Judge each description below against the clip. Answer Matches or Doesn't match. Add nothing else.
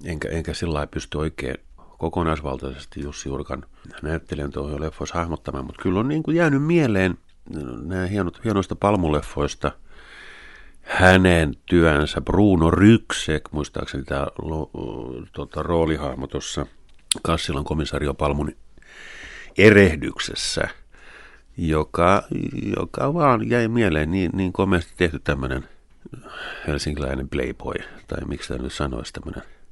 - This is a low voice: Matches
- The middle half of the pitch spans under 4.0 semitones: Doesn't match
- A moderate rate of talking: Matches